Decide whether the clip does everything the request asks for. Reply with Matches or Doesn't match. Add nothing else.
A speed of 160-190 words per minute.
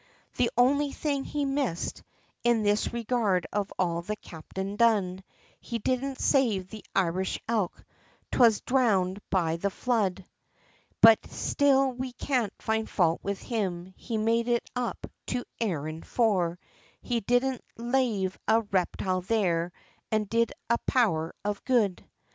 Doesn't match